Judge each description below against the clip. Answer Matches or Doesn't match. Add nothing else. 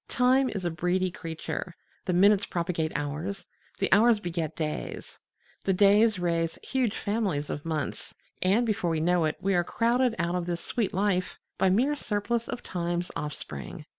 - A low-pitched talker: Doesn't match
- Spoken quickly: Doesn't match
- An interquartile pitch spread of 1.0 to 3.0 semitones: Doesn't match